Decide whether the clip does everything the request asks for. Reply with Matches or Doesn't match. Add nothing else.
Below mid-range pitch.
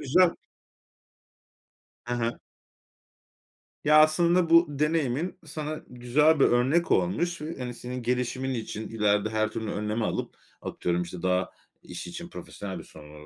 Matches